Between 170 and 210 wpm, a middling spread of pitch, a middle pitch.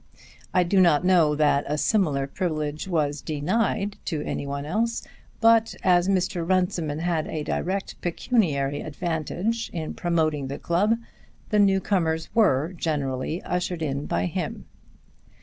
No: average, 140 wpm; average, 4.2 semitones; medium, 165 Hz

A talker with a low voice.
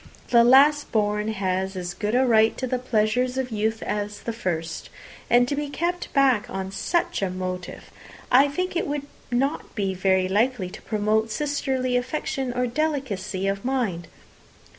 No: high, 230 Hz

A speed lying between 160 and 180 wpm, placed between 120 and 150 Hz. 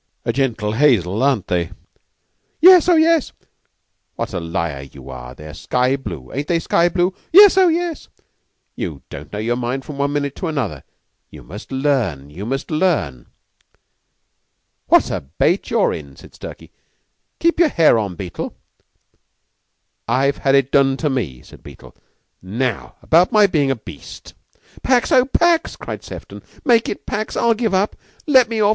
Yes: average, 165 wpm; low, 135 Hz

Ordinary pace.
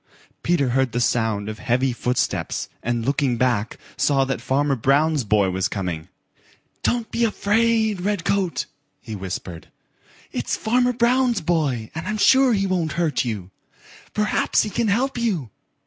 Yes: average, 150 wpm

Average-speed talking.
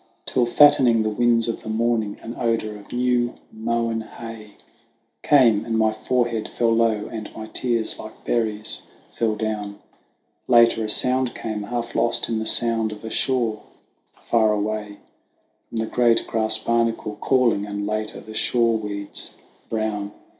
Yes: average, 155 wpm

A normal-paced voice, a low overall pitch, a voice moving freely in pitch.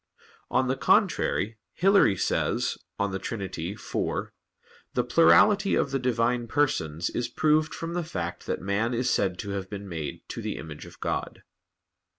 Yes: average, 160 wpm; low, 110 Hz; wide, 6.2 semitones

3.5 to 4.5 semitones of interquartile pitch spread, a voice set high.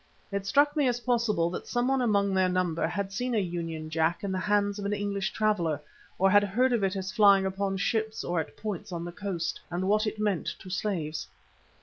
No: average, 2.9 semitones; high, 200 Hz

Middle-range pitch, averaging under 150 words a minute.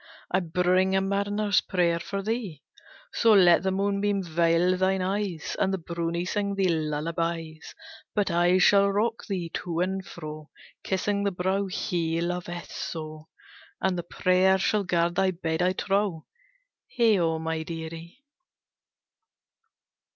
Yes: medium, 180 Hz; slow, 135 wpm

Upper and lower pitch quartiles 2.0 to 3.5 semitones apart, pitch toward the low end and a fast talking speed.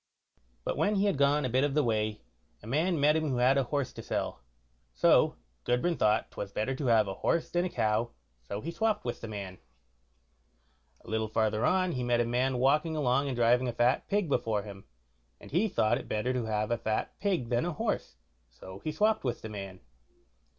No: wide, 5.6 semitones; low, 125 Hz; fast, 215 wpm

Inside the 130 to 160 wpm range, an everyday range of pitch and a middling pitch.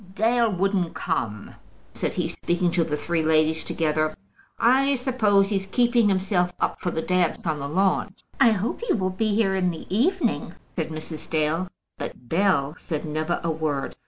No: average, 175 wpm; average, 4.5 semitones; medium, 180 Hz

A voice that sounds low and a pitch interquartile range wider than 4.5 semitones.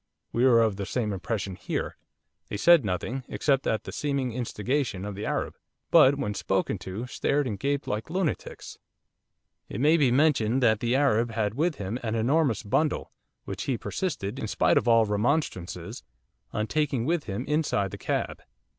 Yes: low, 120 Hz; average, 5.3 semitones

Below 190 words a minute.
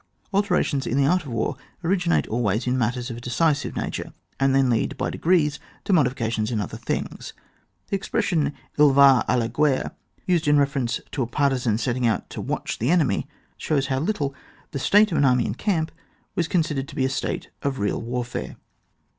No: average, 195 wpm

